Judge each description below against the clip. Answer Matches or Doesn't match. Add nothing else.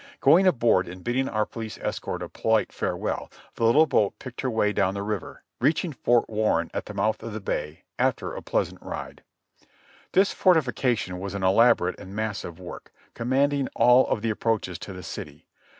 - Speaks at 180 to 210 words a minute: Matches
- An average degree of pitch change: Matches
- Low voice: Matches